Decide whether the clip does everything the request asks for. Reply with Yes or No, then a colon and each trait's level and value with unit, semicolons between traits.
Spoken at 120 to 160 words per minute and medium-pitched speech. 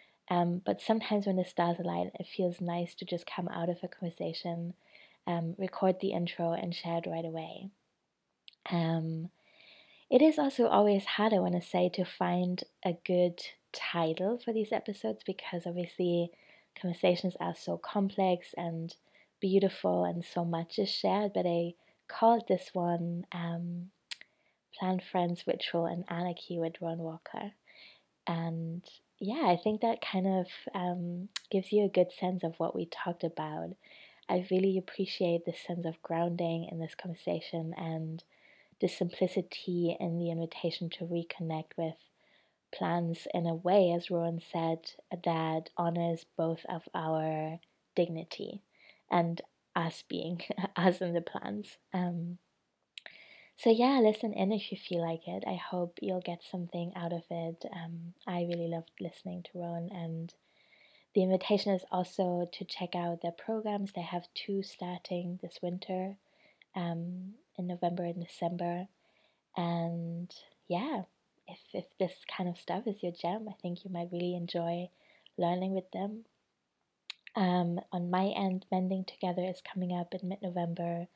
Yes: average, 150 wpm; medium, 175 Hz